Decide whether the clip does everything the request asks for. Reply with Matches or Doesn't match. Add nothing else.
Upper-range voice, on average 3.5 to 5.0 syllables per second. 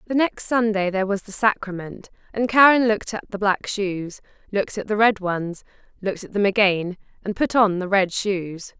Doesn't match